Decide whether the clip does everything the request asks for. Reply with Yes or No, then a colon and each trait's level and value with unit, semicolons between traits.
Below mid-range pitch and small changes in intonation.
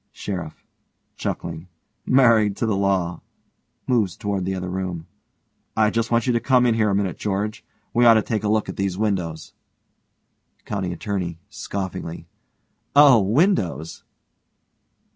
No: low, 100 Hz; average, 3.7 semitones